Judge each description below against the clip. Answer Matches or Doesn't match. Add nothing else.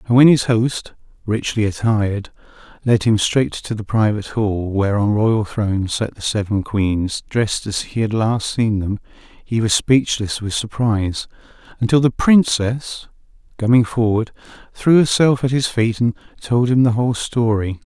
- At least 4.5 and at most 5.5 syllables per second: Matches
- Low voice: Matches